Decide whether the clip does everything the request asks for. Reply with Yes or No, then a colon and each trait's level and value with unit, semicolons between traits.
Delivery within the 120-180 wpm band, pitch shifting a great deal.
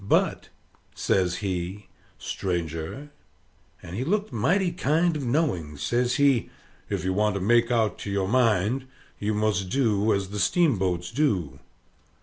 Yes: average, 140 wpm; wide, 6.1 semitones